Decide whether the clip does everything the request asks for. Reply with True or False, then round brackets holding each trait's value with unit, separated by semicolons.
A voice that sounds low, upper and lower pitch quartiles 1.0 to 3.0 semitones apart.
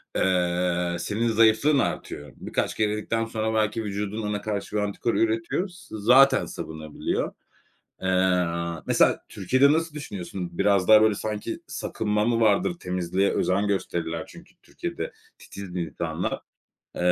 False (105 Hz; 3.6 semitones)